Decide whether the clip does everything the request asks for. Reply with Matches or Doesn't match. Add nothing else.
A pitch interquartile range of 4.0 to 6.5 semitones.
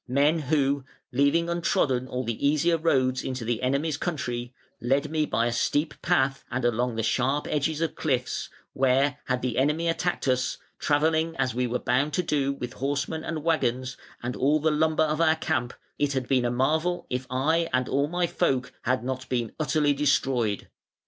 Doesn't match